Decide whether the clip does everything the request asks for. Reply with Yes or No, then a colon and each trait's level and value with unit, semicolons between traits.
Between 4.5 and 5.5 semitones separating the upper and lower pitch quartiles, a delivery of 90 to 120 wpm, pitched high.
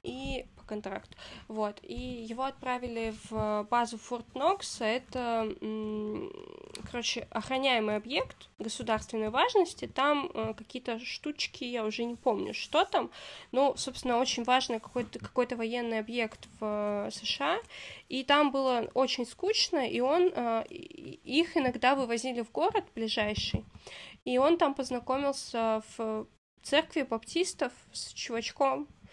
No: average, 3.8 semitones; average, 115 wpm; high, 245 Hz